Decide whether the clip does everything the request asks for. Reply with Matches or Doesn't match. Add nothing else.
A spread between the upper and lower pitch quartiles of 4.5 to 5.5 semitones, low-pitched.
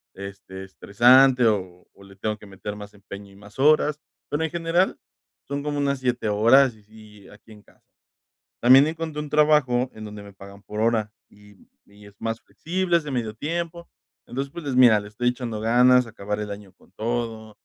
Matches